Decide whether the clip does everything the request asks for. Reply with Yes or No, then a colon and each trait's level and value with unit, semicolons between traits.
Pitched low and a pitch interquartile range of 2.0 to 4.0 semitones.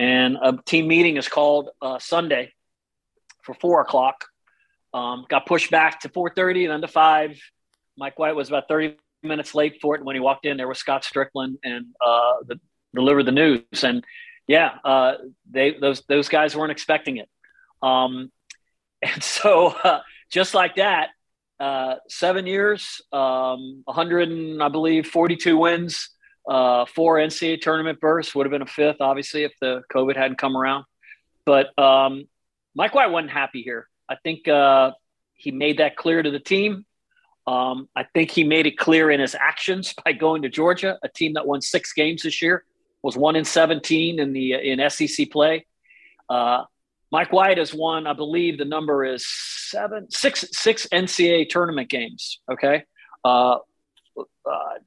No: medium, 150 Hz; average, 3.7 semitones